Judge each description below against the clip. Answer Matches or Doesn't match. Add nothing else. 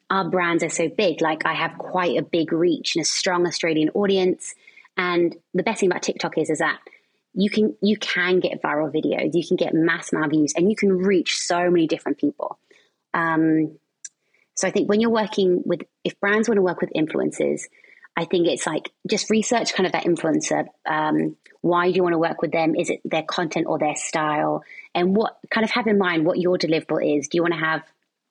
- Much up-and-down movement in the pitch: Doesn't match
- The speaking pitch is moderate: Matches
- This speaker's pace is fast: Matches